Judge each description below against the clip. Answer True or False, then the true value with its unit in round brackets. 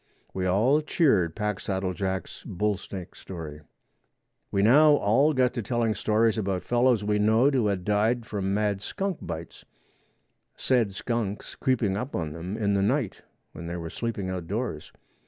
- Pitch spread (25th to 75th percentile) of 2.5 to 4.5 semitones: True (4.1 semitones)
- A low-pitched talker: True (105 Hz)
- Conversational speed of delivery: True (155 wpm)